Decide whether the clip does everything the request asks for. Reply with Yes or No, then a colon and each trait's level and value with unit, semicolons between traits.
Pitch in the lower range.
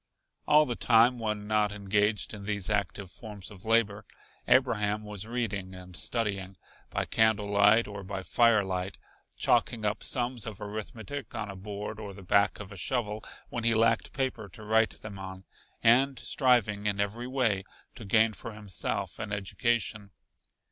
Yes: low, 105 Hz